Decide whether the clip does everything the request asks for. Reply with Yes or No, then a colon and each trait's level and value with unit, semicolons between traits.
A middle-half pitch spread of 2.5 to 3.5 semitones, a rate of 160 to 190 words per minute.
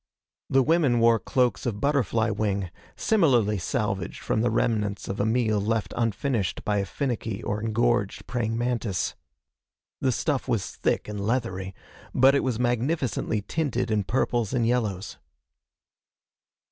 No: average, 3.2 semitones; average, 140 wpm